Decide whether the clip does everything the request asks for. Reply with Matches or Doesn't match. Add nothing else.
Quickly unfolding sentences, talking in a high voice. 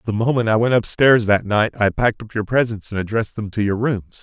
Doesn't match